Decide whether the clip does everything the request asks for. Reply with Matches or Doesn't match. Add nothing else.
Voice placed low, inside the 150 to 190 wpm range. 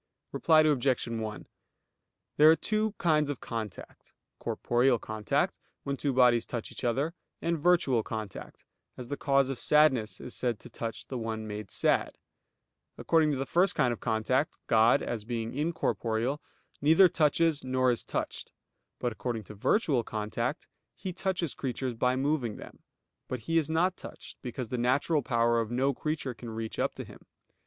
Matches